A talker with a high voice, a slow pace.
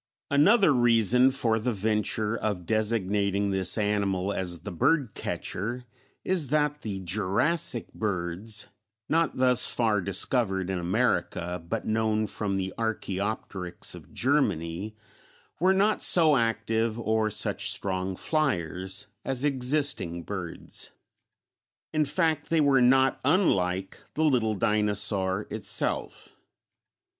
No: low, 110 Hz; slow, 115 wpm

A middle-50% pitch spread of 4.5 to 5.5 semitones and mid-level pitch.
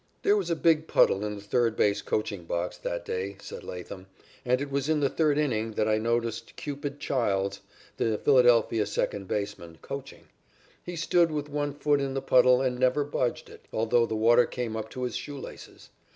No: average, 5.1 semitones; low, 120 Hz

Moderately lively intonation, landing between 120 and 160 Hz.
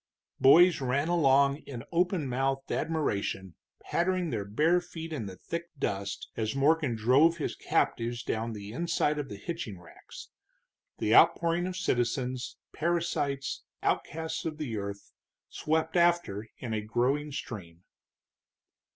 No: wide, 6.4 semitones; medium, 140 Hz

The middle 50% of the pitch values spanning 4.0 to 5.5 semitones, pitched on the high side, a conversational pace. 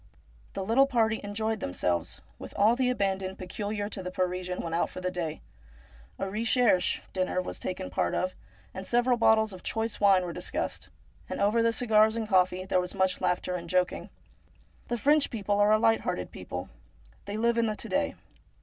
No: average, 3.5 semitones; high, 200 Hz; average, 185 wpm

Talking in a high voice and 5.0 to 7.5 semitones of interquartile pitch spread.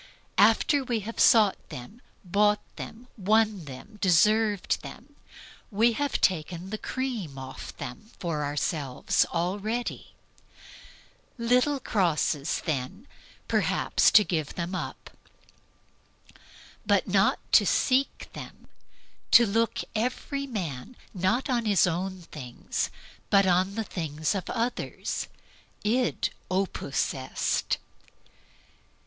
Yes: high, 200 Hz; wide, 5.4 semitones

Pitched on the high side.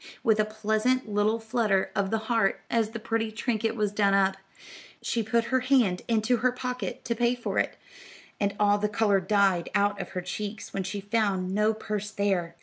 Yes: high, 215 Hz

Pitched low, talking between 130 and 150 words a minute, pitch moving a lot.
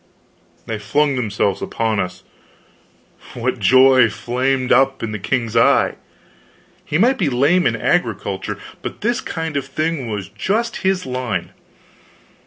Yes: low, 130 Hz; average, 140 wpm; wide, 5.8 semitones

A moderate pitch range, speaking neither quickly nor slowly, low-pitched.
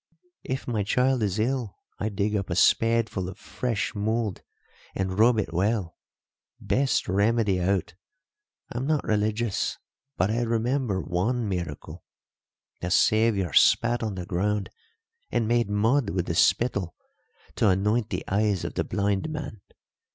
Yes: average, 3.5 semitones; average, 145 wpm; low, 105 Hz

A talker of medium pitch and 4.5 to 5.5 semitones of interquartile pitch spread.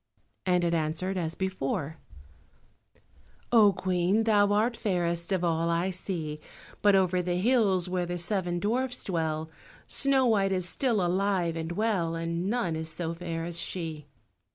No: medium, 180 Hz; average, 3.3 semitones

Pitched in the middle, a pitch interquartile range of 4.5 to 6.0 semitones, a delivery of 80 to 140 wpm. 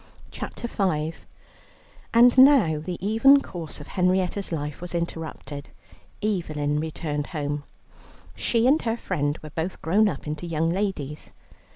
Yes: medium, 170 Hz; average, 5.3 semitones; slow, 135 wpm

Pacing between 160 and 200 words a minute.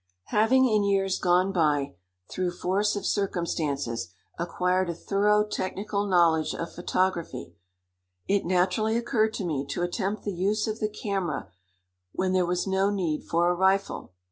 No: average, 150 wpm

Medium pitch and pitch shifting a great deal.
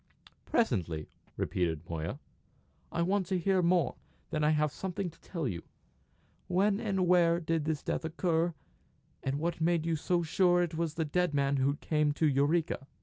No: medium, 165 Hz; average, 3.4 semitones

